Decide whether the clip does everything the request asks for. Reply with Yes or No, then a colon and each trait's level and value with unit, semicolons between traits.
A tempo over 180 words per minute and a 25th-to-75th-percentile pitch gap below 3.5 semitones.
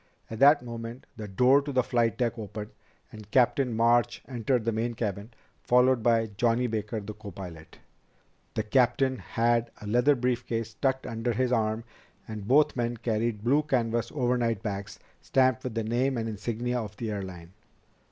No: average, 170 wpm; narrow, 2.5 semitones